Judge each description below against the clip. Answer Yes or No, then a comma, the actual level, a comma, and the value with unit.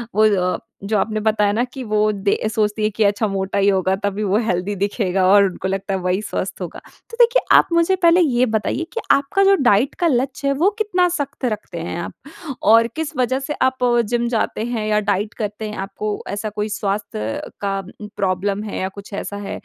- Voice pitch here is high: Yes, high, 215 Hz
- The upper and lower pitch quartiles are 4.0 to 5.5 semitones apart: Yes, average, 4.3 semitones